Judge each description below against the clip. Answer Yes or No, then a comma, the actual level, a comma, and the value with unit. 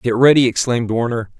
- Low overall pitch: Yes, low, 120 Hz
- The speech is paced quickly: No, average, 170 wpm